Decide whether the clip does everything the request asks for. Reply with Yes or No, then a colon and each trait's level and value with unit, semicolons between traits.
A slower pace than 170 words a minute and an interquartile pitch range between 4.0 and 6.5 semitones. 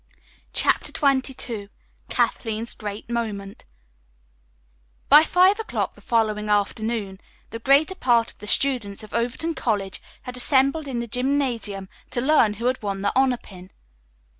Yes: average, 140 wpm; average, 4.3 semitones